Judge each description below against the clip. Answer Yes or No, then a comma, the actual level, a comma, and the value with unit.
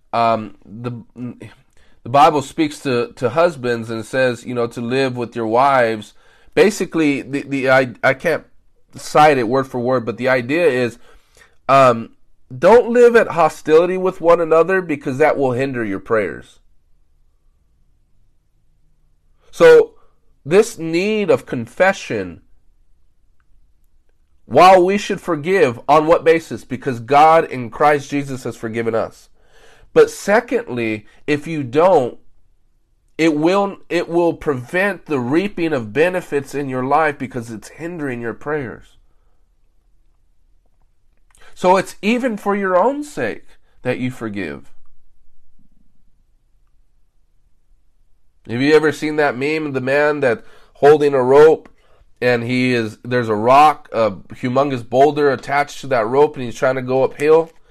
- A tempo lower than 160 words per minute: Yes, slow, 135 wpm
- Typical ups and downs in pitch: No, wide, 5.8 semitones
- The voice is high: No, low, 135 Hz